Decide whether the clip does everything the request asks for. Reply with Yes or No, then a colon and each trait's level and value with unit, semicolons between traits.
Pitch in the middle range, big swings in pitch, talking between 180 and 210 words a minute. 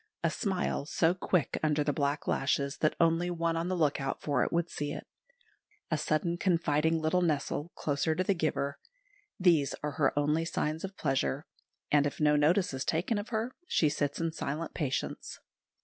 No: medium, 155 Hz; average, 2.8 semitones; average, 185 wpm